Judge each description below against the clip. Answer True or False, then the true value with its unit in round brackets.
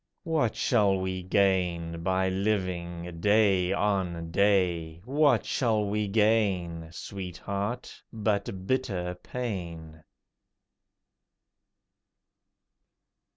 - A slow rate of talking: True (75 wpm)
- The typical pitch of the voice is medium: False (95 Hz)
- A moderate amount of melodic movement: True (3.3 semitones)